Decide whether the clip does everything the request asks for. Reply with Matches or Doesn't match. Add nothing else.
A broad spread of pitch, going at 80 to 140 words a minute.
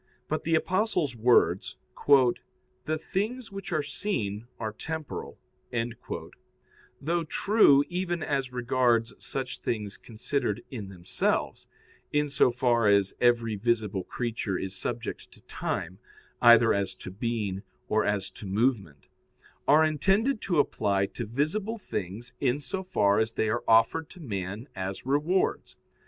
Matches